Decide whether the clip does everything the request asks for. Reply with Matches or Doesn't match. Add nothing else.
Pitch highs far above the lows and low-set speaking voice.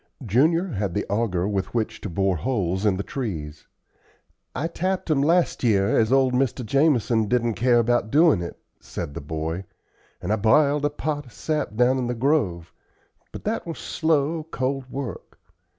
Matches